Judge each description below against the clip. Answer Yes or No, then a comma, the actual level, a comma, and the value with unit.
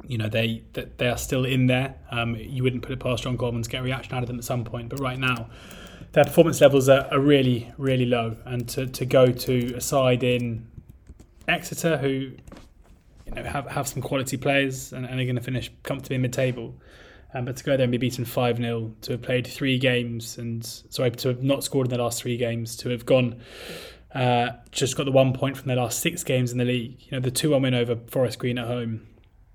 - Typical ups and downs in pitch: No, narrow, 1.9 semitones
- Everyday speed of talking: No, fast, 235 wpm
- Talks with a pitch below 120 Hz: No, low, 125 Hz